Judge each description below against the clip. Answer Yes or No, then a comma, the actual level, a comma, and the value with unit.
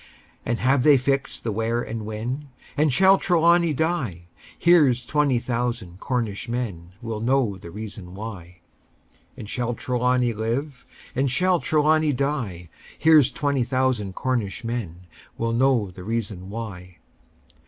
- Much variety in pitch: No, average, 4.5 semitones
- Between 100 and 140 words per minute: Yes, slow, 135 wpm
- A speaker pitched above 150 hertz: No, low, 120 Hz